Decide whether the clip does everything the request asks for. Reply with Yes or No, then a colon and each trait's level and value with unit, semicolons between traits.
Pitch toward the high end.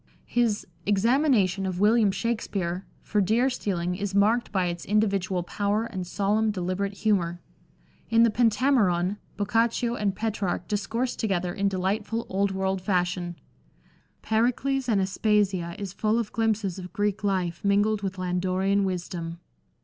Yes: high, 200 Hz